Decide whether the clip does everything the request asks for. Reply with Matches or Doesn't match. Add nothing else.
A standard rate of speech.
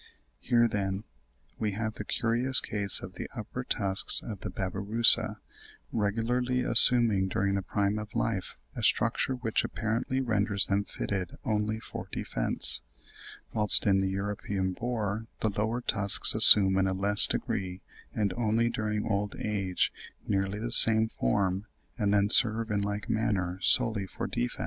Matches